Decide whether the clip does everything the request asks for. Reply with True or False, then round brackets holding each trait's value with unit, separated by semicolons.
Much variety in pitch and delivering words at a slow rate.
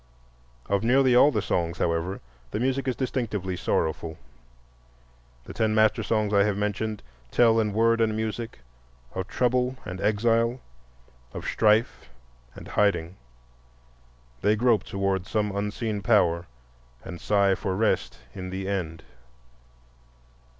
False (3.1 semitones; 130 wpm)